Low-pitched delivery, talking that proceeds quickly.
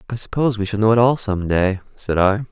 Yes: low, 105 Hz; fast, 260 wpm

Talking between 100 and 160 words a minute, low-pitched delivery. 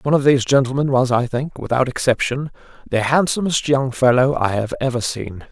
No: average, 185 wpm; low, 130 Hz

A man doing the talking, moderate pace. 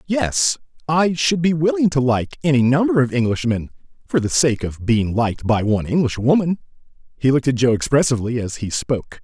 Yes: male; average, 175 wpm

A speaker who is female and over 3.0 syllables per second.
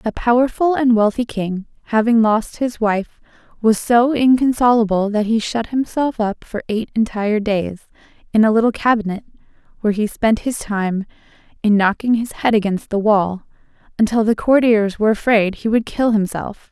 Yes: female; 5.0 syllables/s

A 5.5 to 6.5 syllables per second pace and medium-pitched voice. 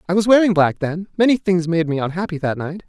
Yes: 6.2 syllables/s; medium, 175 Hz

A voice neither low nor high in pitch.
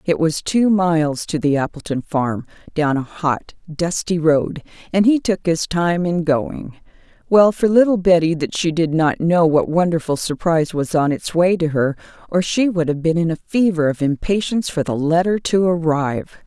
Yes: medium, 165 Hz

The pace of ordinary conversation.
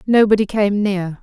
Yes: average, 145 wpm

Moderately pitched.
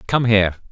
No: low, 105 Hz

